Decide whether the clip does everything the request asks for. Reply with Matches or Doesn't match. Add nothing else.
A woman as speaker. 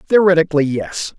Doesn't match